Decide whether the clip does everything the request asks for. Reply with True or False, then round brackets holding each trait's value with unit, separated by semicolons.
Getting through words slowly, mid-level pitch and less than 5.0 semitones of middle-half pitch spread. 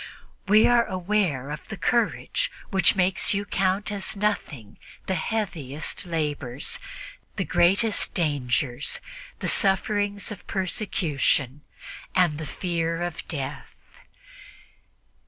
False (105 wpm; 180 Hz; 5.5 semitones)